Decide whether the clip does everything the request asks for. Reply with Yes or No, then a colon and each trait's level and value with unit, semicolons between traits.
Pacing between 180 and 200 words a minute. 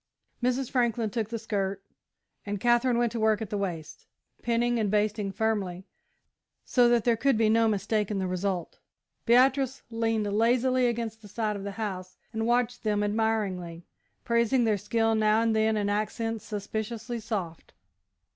No: average, 165 wpm